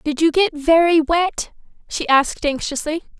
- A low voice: No, very high, 315 Hz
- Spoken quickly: No, average, 150 wpm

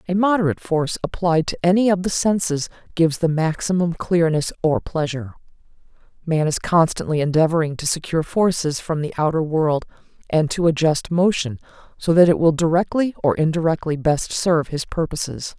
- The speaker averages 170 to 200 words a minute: No, average, 160 wpm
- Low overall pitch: No, medium, 165 Hz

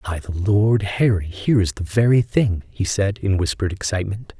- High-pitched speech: No, low, 100 Hz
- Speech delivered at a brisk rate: No, average, 190 wpm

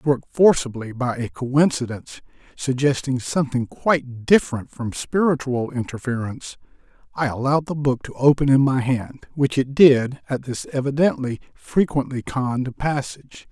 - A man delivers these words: Yes, male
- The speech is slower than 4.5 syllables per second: No, 4.9 syllables/s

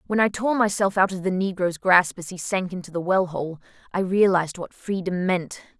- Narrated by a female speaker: Yes, female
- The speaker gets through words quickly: Yes, fast, 215 wpm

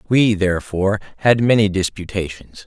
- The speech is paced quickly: No, slow, 110 wpm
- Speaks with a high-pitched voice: No, low, 100 Hz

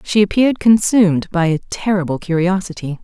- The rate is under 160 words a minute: Yes, average, 140 wpm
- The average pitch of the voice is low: No, high, 190 Hz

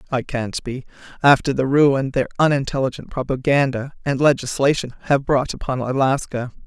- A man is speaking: No, female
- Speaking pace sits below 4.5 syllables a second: No, 5.2 syllables/s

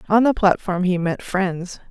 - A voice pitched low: No, high, 190 Hz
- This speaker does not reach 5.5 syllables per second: Yes, 4.3 syllables/s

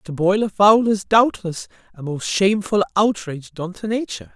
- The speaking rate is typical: Yes, average, 180 wpm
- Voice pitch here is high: Yes, high, 195 Hz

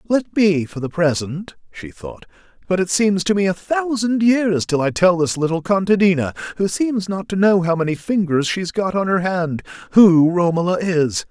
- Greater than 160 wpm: Yes, average, 195 wpm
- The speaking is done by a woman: No, male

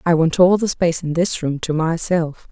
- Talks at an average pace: No, fast, 240 wpm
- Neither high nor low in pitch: Yes, medium, 170 Hz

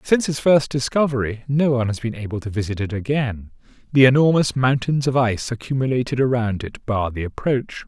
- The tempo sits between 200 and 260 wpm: No, average, 185 wpm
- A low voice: Yes, low, 125 Hz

